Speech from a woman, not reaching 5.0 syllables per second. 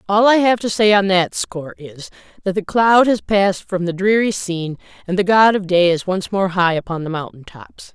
No: female; 5.2 syllables/s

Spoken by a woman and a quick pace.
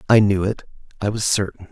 No: male; fast, 210 wpm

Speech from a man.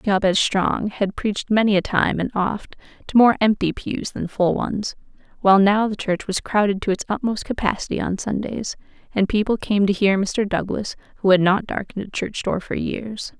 No: female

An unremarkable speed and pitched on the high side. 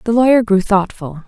Yes: average, 190 wpm; high, 210 Hz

